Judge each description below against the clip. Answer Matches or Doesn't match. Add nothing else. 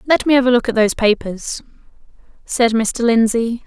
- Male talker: Doesn't match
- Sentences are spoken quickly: Doesn't match